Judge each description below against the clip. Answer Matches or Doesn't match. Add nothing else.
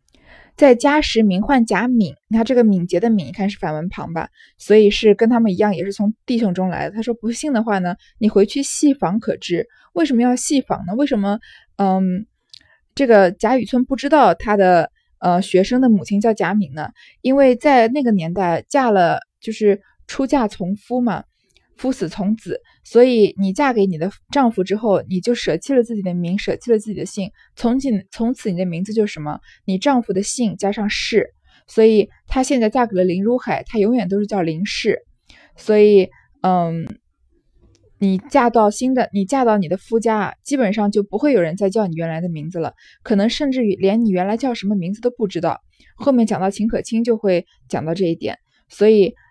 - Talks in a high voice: Matches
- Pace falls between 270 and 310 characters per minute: Matches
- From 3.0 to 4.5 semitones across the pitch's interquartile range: Matches